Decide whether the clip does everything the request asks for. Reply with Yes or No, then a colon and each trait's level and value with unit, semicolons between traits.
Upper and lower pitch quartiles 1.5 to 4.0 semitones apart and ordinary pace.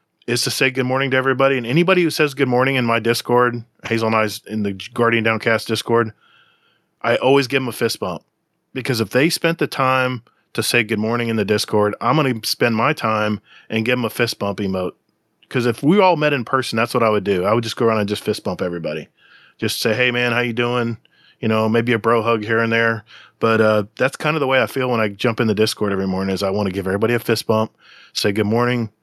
No: average, 2.8 semitones; fast, 255 wpm